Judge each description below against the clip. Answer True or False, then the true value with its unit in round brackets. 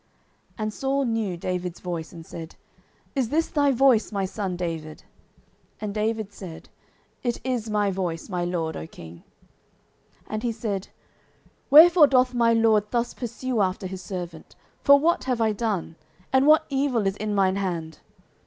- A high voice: True (210 Hz)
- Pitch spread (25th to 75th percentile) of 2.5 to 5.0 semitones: False (5.5 semitones)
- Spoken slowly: False (165 wpm)